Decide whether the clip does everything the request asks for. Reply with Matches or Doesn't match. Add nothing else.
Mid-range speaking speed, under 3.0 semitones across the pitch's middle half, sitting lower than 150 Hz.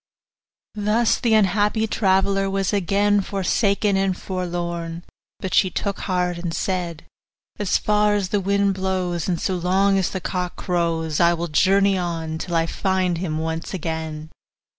Doesn't match